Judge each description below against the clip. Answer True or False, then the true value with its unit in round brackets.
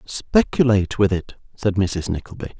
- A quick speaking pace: False (140 wpm)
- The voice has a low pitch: True (105 Hz)